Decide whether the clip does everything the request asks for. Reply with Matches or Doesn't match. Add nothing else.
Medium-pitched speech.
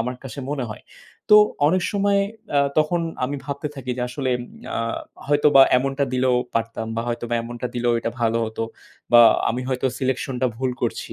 Doesn't match